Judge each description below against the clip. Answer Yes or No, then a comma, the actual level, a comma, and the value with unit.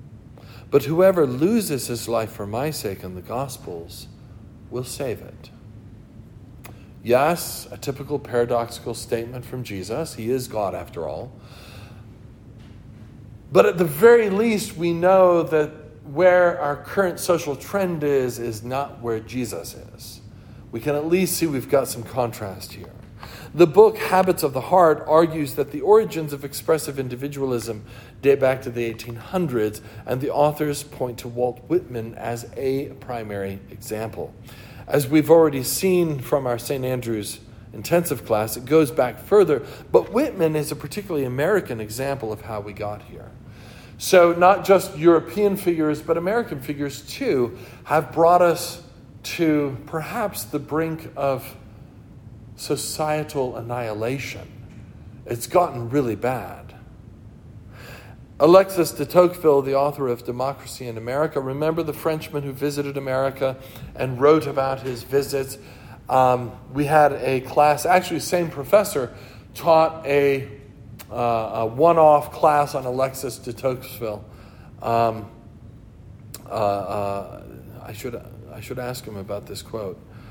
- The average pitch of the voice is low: Yes, low, 130 Hz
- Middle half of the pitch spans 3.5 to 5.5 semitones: Yes, average, 4.8 semitones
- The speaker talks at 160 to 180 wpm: No, average, 140 wpm